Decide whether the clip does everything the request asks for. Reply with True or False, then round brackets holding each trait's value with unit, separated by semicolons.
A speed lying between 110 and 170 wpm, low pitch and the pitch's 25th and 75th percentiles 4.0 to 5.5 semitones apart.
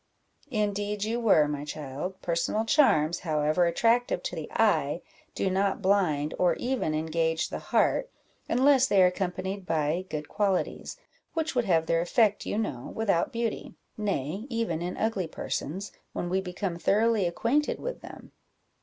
False (155 wpm; 190 Hz; 5.1 semitones)